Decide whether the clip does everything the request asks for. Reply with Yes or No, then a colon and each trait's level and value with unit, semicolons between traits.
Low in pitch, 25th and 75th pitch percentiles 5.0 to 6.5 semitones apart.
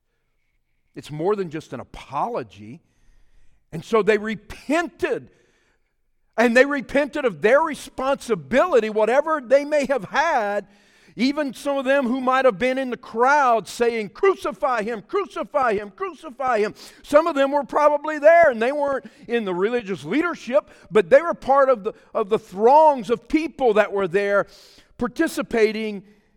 No: high, 245 Hz; wide, 5.6 semitones